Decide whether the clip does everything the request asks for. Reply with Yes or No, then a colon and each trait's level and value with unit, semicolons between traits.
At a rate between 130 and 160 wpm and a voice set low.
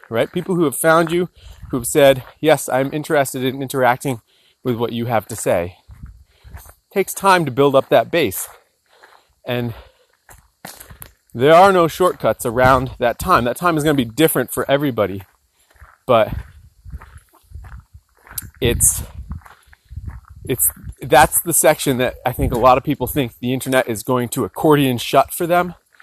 Yes: average, 155 wpm; low, 130 Hz